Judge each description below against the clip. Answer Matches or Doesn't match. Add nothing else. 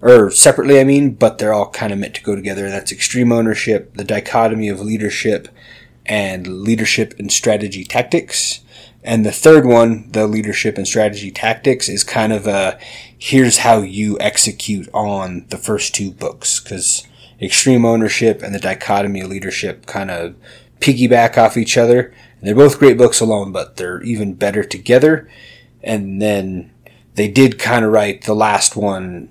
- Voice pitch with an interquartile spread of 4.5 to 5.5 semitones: Doesn't match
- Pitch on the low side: Matches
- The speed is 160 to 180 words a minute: Matches